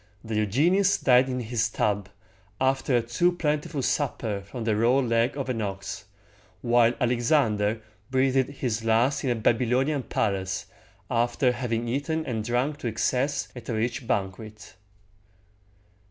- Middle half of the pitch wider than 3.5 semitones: No, average, 3.2 semitones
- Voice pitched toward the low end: Yes, low, 120 Hz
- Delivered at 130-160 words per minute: Yes, average, 150 wpm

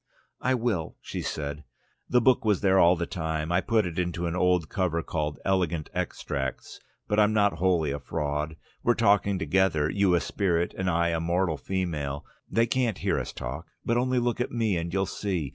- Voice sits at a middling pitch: No, very low, 90 Hz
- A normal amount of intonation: Yes, average, 4.1 semitones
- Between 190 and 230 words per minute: Yes, average, 195 wpm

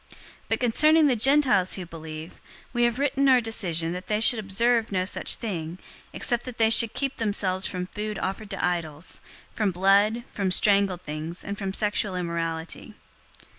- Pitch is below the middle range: No, high, 200 Hz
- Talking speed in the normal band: Yes, average, 170 wpm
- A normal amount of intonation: Yes, average, 4.4 semitones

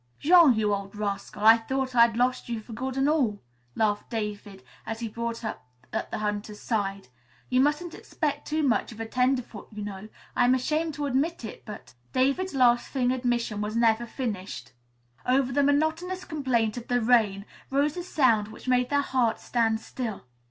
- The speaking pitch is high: Yes, high, 240 Hz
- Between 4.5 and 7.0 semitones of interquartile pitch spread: No, average, 3.9 semitones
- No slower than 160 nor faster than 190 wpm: Yes, average, 180 wpm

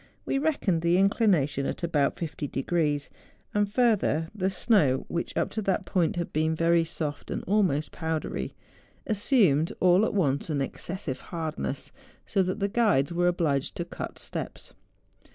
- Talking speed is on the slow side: No, average, 165 wpm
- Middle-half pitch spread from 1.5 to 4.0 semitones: No, average, 4.5 semitones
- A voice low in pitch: No, medium, 170 Hz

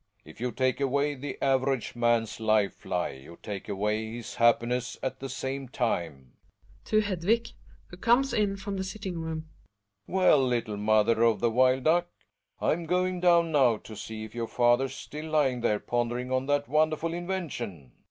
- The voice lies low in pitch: Yes, low, 130 Hz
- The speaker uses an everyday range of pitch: No, wide, 6.3 semitones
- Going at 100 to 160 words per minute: No, average, 175 wpm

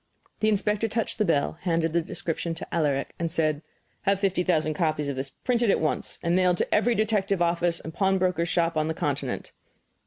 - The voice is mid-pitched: Yes, medium, 170 Hz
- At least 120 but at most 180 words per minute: No, average, 195 wpm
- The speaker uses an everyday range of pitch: Yes, average, 3.7 semitones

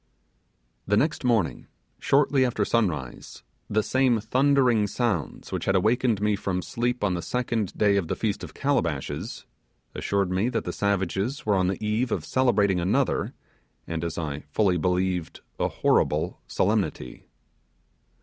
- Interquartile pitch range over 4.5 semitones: Yes, average, 5.0 semitones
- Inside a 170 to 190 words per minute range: No, average, 150 wpm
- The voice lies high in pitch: No, low, 105 Hz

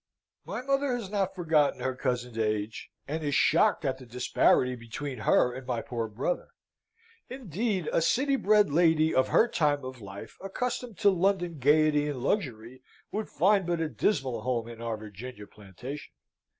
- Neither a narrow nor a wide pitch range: No, wide, 7.4 semitones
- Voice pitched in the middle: Yes, medium, 145 Hz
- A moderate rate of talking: Yes, average, 165 wpm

